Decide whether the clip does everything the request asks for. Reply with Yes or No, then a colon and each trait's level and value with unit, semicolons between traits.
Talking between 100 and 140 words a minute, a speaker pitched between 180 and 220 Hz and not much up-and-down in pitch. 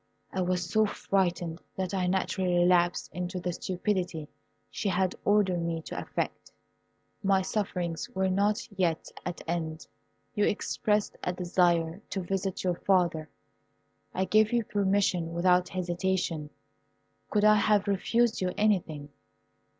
Yes: slow, 135 wpm; medium, 185 Hz; narrow, 2.3 semitones